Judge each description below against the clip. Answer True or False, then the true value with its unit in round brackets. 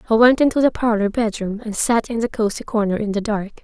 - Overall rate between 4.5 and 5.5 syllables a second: False (6.0 syllables/s)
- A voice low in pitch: False (220 Hz)